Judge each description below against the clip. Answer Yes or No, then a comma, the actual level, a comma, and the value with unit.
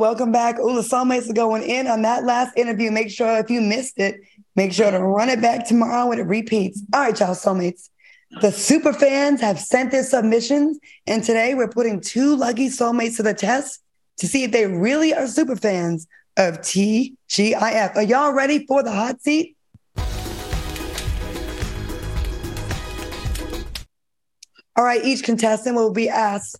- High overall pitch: Yes, high, 230 Hz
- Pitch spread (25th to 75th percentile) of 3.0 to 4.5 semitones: Yes, average, 3.8 semitones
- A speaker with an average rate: Yes, average, 170 wpm